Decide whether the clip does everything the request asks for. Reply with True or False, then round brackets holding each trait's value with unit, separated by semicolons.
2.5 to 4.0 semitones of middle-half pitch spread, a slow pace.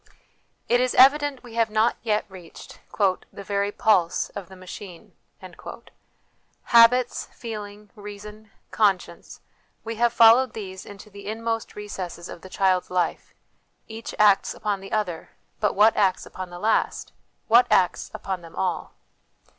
False (3.0 semitones; 145 wpm)